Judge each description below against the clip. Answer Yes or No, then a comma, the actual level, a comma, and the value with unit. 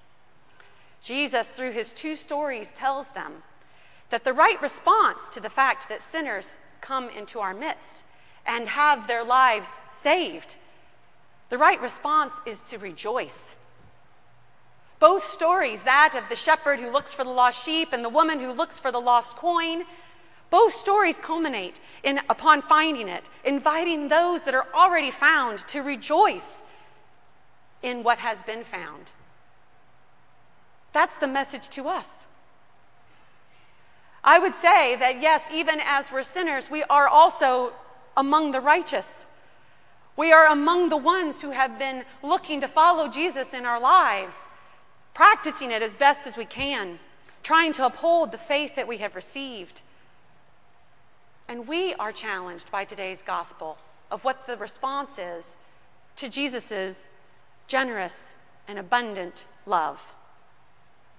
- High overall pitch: Yes, very high, 275 Hz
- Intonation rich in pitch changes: No, average, 4.7 semitones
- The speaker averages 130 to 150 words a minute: Yes, average, 140 wpm